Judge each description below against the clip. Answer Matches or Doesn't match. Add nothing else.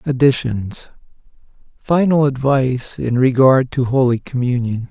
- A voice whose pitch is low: Matches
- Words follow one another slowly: Matches